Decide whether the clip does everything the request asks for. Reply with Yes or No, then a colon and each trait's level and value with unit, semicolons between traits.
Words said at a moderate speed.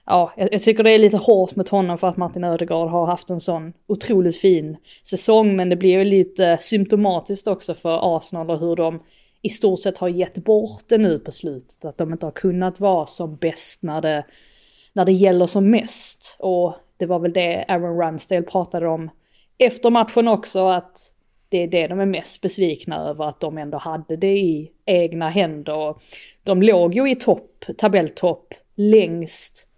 Yes: average, 190 wpm